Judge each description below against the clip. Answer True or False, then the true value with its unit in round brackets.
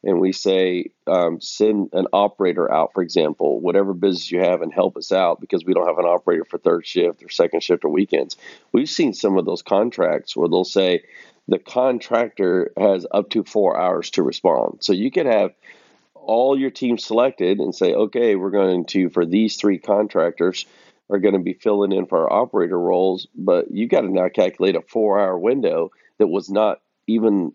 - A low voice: True (120 Hz)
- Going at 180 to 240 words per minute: True (200 wpm)